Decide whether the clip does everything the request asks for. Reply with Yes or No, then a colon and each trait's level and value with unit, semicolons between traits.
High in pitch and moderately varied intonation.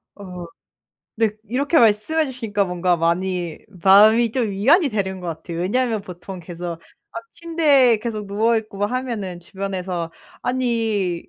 Yes: high, 205 Hz; average, 4.6 semitones